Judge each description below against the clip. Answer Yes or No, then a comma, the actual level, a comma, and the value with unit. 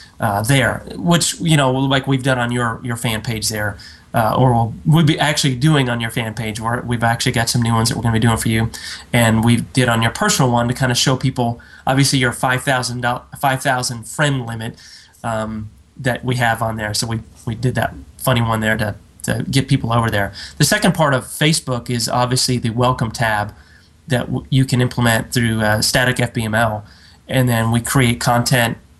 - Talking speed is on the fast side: Yes, fast, 210 wpm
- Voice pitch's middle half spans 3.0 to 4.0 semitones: No, narrow, 2.5 semitones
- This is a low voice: Yes, low, 120 Hz